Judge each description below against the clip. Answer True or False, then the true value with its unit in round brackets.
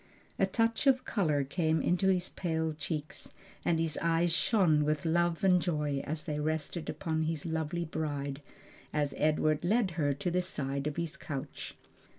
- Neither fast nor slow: True (165 wpm)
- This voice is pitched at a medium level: True (160 Hz)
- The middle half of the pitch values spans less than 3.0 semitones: True (2.6 semitones)